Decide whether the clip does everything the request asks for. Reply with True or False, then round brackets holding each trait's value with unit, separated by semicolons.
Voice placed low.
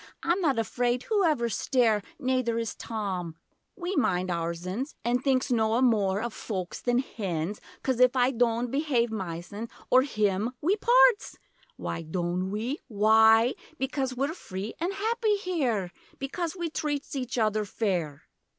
False (235 Hz)